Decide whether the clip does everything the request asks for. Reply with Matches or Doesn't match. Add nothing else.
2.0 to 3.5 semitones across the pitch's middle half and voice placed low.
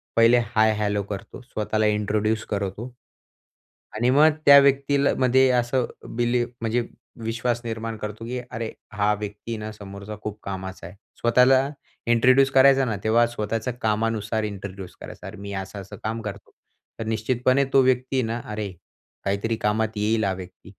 Matches